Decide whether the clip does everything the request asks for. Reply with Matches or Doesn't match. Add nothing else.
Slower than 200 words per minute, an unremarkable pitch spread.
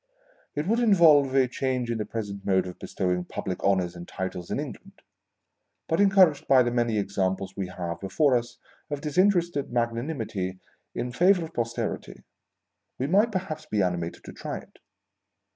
Doesn't match